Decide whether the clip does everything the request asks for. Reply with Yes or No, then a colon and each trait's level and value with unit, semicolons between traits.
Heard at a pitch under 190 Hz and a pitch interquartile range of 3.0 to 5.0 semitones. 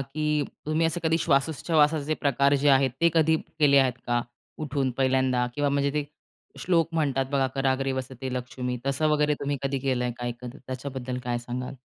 No: low, 135 Hz; narrow, 2.5 semitones